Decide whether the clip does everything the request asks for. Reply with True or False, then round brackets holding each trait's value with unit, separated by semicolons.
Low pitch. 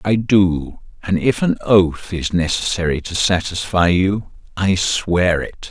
True (90 Hz)